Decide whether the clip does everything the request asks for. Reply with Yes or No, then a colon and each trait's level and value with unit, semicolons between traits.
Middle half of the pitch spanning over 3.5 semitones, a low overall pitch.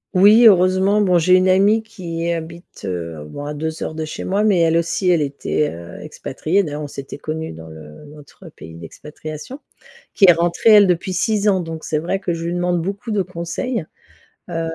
No: average, 3.9 semitones; medium, 170 Hz